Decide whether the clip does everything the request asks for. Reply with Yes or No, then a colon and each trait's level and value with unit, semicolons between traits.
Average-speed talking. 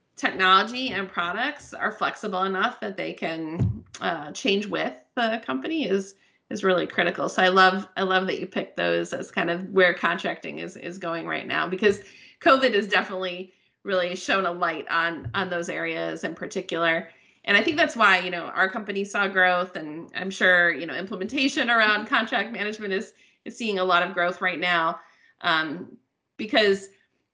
Yes: average, 180 wpm